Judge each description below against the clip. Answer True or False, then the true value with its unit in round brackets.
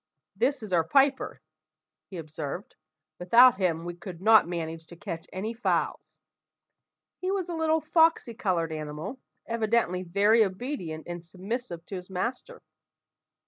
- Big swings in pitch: True (6.4 semitones)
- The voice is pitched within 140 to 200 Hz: True (190 Hz)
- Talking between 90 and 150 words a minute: True (140 wpm)